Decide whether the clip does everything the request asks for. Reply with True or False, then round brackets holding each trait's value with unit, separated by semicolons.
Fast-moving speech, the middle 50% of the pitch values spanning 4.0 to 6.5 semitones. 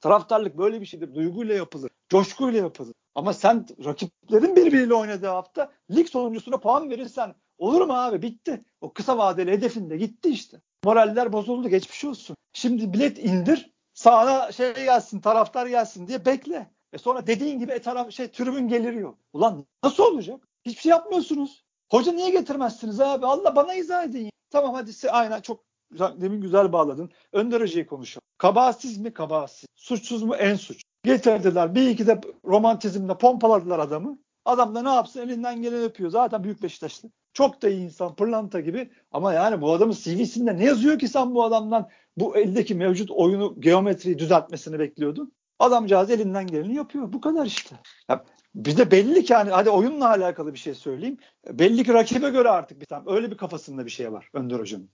True (170 wpm; 5.1 semitones)